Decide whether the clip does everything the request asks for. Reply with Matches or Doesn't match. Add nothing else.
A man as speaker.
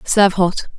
Doesn't match